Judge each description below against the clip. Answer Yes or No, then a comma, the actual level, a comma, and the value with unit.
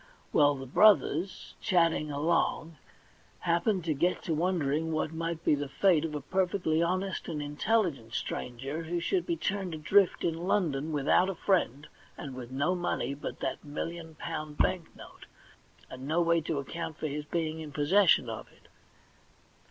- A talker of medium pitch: Yes, medium, 160 Hz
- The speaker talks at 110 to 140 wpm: No, average, 165 wpm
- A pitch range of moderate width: Yes, average, 3.3 semitones